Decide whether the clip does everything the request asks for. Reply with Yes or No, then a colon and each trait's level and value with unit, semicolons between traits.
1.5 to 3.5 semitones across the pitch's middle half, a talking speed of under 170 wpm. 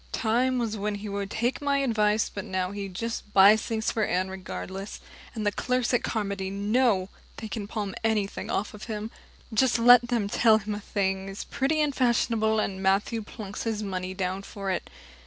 No: average, 2.8 semitones; average, 195 wpm